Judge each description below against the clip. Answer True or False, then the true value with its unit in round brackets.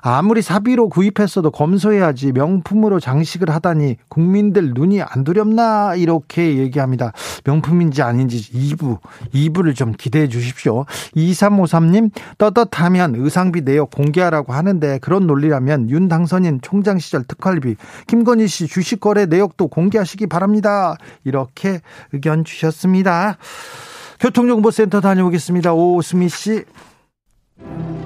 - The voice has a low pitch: False (175 Hz)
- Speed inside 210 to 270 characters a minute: False (305 characters per minute)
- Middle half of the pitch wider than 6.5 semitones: False (5.5 semitones)